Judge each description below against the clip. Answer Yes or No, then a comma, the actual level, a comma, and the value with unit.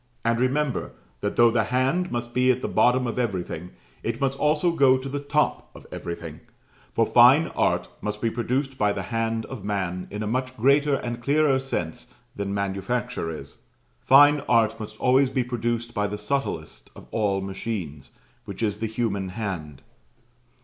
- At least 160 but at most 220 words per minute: Yes, average, 175 wpm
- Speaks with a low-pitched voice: Yes, low, 115 Hz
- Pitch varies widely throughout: No, average, 4.3 semitones